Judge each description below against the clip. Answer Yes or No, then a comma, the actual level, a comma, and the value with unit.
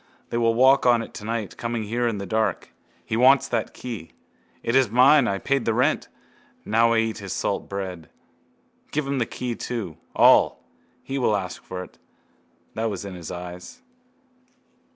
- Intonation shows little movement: No, average, 3.9 semitones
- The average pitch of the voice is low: Yes, low, 115 Hz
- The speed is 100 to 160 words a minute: No, average, 175 wpm